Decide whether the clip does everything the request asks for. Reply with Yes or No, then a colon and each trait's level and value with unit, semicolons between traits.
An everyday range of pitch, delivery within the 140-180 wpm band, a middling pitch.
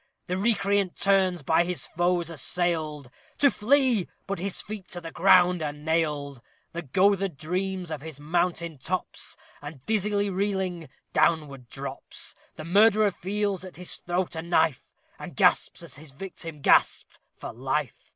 Yes: average, 3.8 semitones; average, 150 wpm; medium, 175 Hz